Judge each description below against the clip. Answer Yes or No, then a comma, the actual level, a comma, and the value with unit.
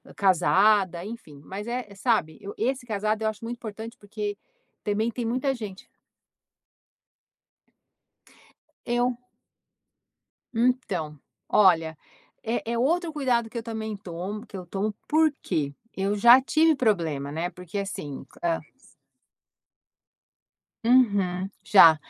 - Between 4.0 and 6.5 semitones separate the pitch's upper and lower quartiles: Yes, average, 4.5 semitones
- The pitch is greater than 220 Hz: No, high, 210 Hz